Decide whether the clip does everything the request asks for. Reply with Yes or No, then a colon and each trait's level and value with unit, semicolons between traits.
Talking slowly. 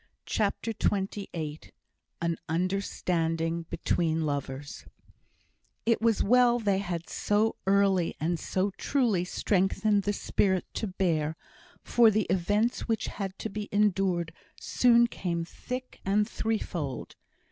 Yes: slow, 115 wpm